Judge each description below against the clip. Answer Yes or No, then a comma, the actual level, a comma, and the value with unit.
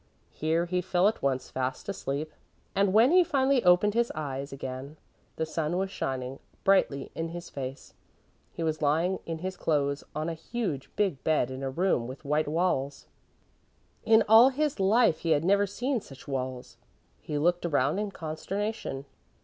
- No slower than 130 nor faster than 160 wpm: No, average, 170 wpm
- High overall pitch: No, medium, 165 Hz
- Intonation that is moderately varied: No, wide, 6.0 semitones